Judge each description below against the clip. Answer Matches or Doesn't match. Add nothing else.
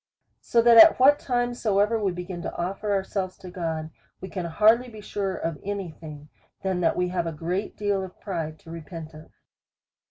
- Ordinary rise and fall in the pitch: Matches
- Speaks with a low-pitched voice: Doesn't match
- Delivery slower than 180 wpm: Doesn't match